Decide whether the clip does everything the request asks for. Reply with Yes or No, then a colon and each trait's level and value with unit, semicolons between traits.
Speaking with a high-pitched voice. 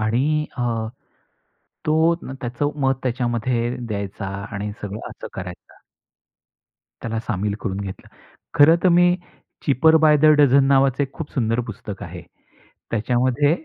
No: low, 125 Hz